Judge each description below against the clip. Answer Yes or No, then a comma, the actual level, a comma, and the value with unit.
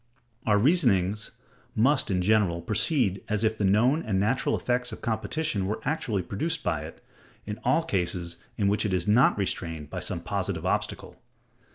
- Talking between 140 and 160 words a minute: No, average, 170 wpm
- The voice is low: Yes, low, 105 Hz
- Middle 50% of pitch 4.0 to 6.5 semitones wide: Yes, average, 4.7 semitones